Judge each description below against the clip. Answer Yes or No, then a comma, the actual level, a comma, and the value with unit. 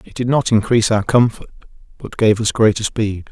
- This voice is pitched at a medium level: No, low, 110 Hz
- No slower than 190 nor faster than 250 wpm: Yes, average, 200 wpm